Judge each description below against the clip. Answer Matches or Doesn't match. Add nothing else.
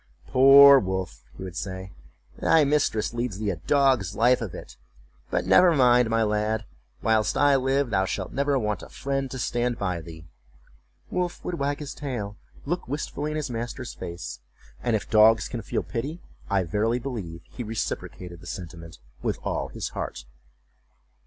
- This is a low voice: Matches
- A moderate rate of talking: Matches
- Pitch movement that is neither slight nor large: Doesn't match